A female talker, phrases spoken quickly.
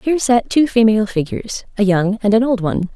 Yes: female; fast, 225 wpm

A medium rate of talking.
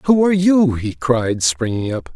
Yes: average, 195 wpm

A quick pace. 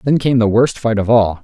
Yes: fast, 290 wpm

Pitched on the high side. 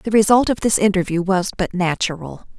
Yes: high, 195 Hz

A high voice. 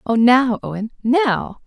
Yes: high, 240 Hz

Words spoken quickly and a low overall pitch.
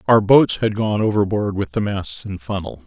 Yes: fast, 210 wpm; low, 105 Hz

